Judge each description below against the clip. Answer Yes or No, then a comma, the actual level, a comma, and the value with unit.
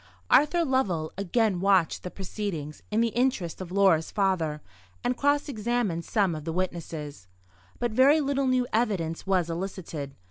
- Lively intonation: Yes, wide, 6.5 semitones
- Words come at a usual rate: Yes, average, 150 wpm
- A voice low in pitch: No, high, 195 Hz